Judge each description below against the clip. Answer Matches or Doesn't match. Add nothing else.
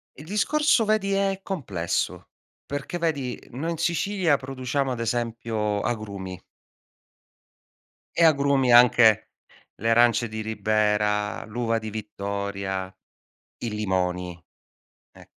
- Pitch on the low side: Matches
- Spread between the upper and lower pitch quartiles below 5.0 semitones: Doesn't match